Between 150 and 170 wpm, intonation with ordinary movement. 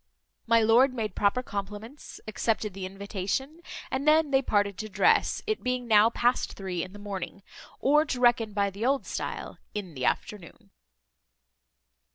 Yes: average, 160 wpm; average, 4.0 semitones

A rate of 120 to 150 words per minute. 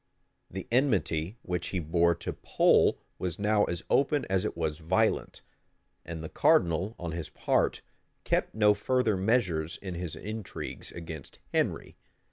Yes: average, 145 wpm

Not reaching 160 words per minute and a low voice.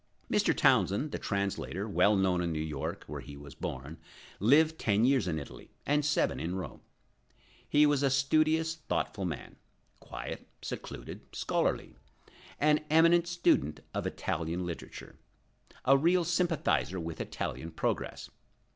Yes: average, 140 wpm; low, 105 Hz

